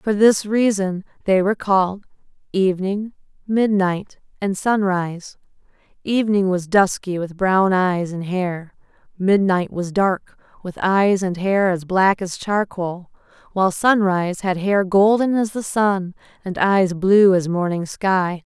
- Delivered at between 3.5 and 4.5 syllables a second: Yes, 4.1 syllables/s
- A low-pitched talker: No, high, 190 Hz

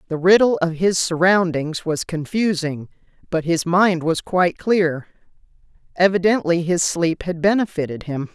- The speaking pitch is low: No, medium, 175 Hz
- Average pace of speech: No, slow, 130 wpm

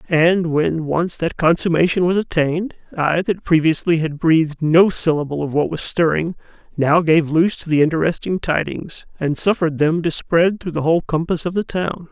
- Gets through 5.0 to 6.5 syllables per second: Yes, 5.1 syllables/s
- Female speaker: No, male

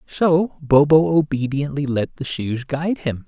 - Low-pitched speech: No, medium, 145 Hz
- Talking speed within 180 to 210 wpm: No, average, 145 wpm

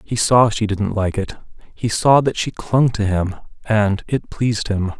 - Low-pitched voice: Yes, low, 110 Hz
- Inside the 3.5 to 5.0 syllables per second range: Yes, 4.2 syllables/s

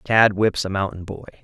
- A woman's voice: No, male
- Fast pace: Yes, fast, 210 wpm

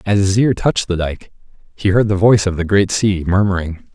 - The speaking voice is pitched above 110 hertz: No, low, 100 Hz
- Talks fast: Yes, fast, 230 wpm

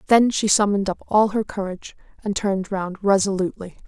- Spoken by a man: No, female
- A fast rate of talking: No, average, 170 wpm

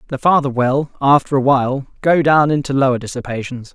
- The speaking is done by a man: Yes, male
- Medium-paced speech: Yes, average, 175 wpm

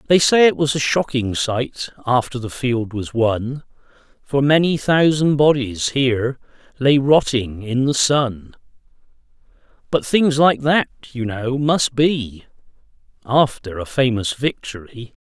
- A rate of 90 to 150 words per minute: Yes, slow, 135 wpm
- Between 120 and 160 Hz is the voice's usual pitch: Yes, low, 130 Hz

